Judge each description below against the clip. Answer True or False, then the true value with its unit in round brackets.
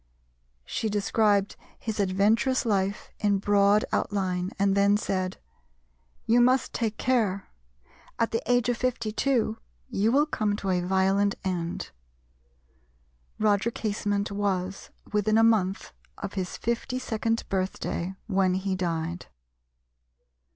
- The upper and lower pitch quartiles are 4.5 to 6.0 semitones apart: False (2.8 semitones)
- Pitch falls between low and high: False (205 Hz)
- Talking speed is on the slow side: True (120 wpm)